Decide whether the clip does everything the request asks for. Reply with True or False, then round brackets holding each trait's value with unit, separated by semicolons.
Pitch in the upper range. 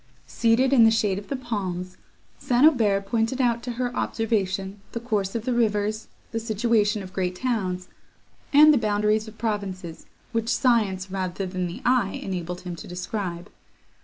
True (210 Hz)